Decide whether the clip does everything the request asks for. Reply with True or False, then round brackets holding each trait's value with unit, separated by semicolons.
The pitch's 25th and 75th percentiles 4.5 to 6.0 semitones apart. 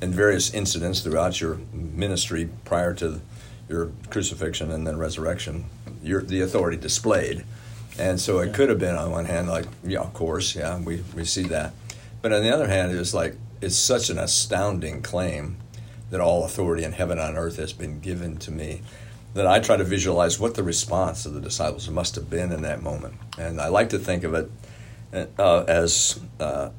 True (4.8 semitones)